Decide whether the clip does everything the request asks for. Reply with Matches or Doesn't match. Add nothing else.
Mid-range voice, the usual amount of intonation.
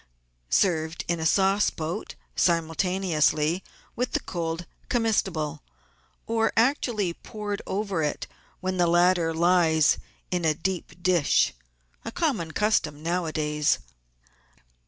Matches